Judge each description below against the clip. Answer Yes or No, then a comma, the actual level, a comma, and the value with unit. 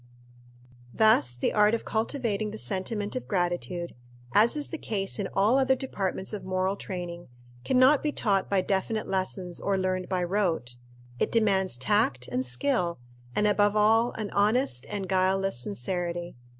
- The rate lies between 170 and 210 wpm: No, average, 160 wpm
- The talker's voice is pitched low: No, high, 195 Hz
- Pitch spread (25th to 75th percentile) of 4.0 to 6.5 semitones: No, average, 3.3 semitones